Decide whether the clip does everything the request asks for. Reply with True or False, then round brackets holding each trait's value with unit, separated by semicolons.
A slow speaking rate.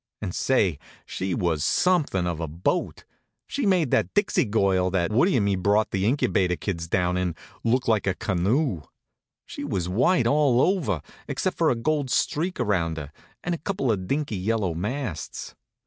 False (175 wpm)